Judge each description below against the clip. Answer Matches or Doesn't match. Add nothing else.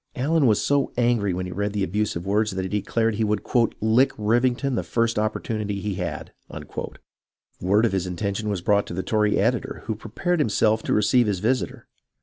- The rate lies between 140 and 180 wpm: Doesn't match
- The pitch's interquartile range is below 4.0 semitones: Matches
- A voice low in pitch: Matches